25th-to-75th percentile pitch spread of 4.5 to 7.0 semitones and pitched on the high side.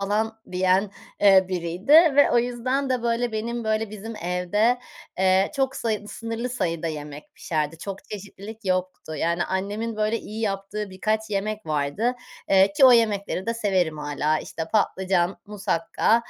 No: average, 3.6 semitones; high, 205 Hz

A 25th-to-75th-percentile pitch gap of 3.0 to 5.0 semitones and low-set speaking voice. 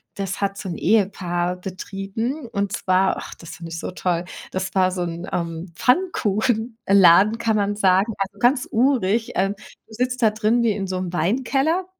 No: average, 3.7 semitones; high, 200 Hz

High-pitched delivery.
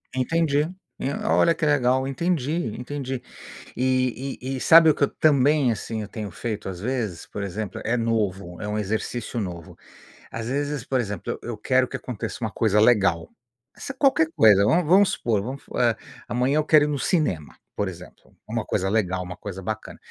No: low, 120 Hz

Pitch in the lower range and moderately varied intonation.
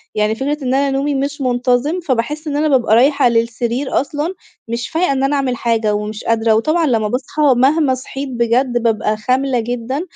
No: very high, 255 Hz; average, 3.4 semitones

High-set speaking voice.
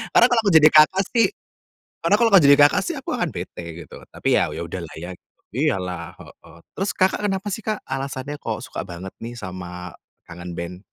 No: medium, 140 Hz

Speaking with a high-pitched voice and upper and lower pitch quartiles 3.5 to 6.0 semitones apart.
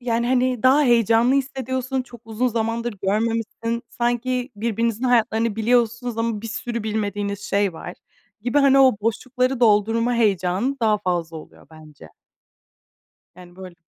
No: high, 230 Hz; average, 3.0 semitones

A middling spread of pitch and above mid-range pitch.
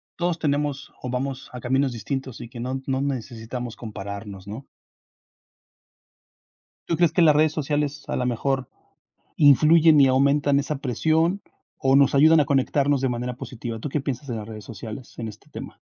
No: average, 3.4 semitones; low, 135 Hz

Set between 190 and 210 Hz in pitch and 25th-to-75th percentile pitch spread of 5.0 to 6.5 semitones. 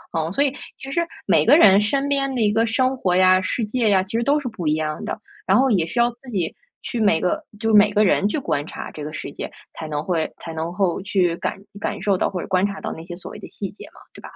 Yes: high, 200 Hz; average, 5.3 semitones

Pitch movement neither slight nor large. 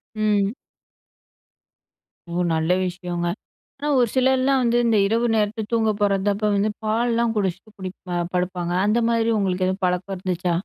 Yes: average, 3.9 semitones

